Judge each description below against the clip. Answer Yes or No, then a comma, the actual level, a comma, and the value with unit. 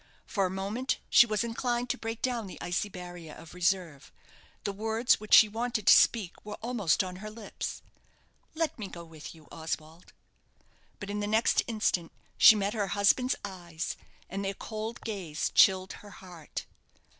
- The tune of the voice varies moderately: Yes, average, 3.8 semitones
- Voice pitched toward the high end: Yes, high, 200 Hz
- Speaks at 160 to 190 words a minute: Yes, average, 170 wpm